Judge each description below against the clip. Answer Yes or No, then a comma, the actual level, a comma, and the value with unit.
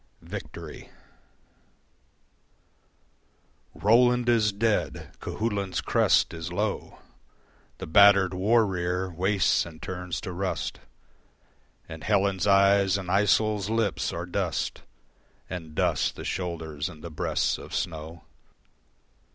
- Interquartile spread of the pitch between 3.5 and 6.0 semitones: No, average, 2.9 semitones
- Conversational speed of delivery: No, slow, 105 wpm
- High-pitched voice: No, very low, 95 Hz